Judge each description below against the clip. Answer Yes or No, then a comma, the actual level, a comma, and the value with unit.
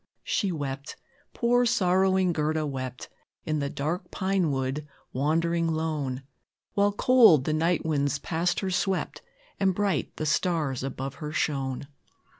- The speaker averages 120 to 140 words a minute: Yes, slow, 135 wpm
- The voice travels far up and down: No, average, 4.9 semitones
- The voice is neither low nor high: Yes, medium, 160 Hz